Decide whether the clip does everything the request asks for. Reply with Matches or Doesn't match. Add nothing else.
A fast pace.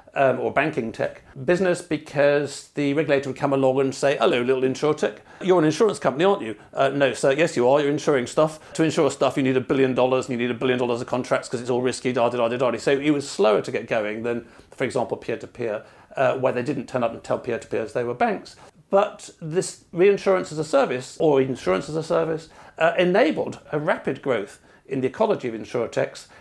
Matches